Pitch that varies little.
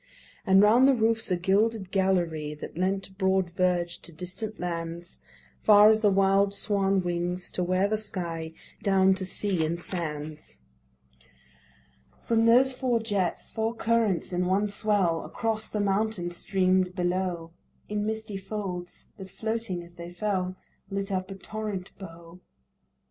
No: average, 3.0 semitones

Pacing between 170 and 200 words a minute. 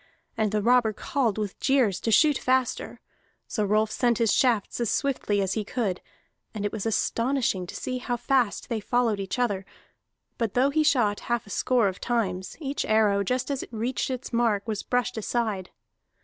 Yes: average, 190 wpm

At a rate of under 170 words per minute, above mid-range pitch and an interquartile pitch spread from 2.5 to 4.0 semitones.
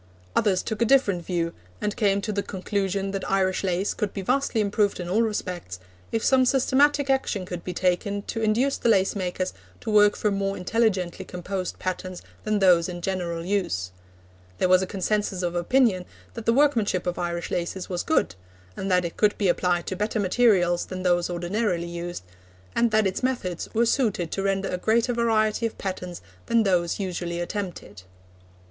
No: average, 185 wpm; high, 195 Hz; average, 3.4 semitones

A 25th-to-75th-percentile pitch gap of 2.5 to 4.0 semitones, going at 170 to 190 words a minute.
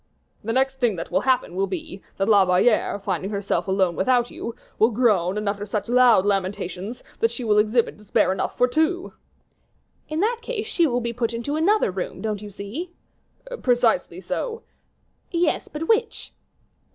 No: average, 5.1 semitones; average, 175 wpm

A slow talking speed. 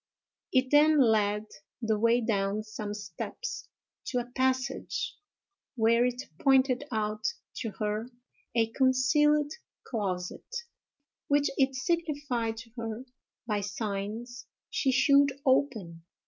Yes: slow, 110 wpm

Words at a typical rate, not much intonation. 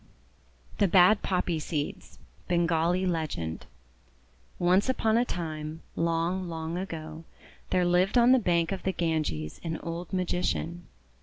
No: slow, 130 wpm; narrow, 2.3 semitones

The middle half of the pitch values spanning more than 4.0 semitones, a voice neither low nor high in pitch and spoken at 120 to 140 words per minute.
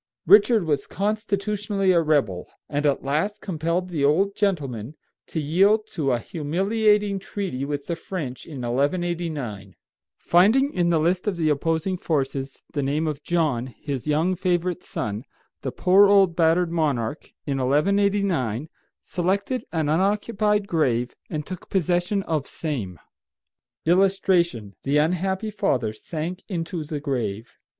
Yes: average, 5.3 semitones; medium, 165 Hz; slow, 135 wpm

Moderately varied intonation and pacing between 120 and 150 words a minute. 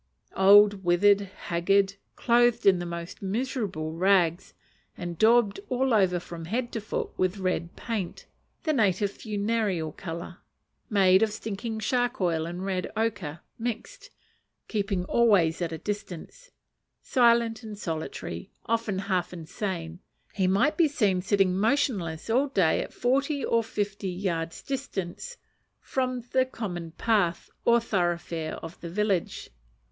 Yes: average, 4.7 semitones; slow, 135 wpm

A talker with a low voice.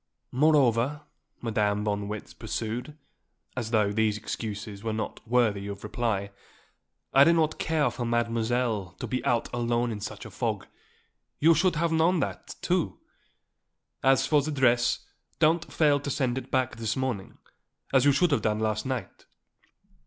Yes: low, 120 Hz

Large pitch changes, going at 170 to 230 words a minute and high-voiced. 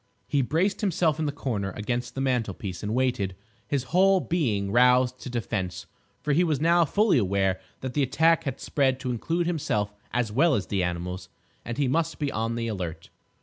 No: wide, 6.8 semitones; average, 190 wpm; low, 125 Hz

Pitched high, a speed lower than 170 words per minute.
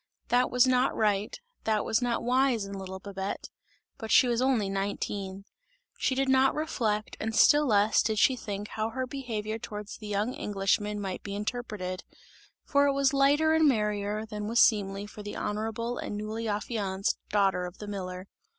No: high, 215 Hz; average, 180 wpm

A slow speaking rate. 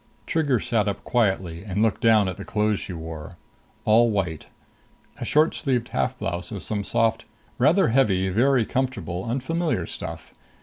No: average, 160 wpm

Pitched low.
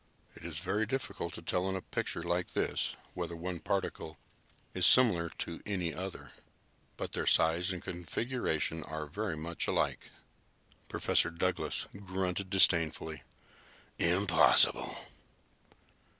Yes: very low, 90 Hz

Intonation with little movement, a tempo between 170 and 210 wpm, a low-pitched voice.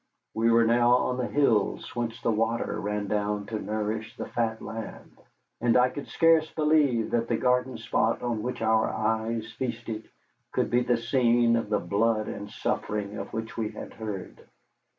Yes: narrow, 1.9 semitones; average, 175 wpm; low, 115 Hz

